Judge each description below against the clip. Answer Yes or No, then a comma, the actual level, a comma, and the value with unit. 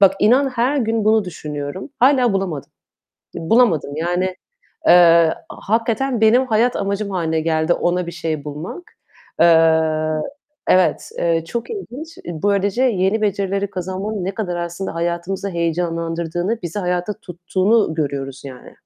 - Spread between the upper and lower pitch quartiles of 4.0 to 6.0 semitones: Yes, average, 4.6 semitones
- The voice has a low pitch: No, medium, 185 Hz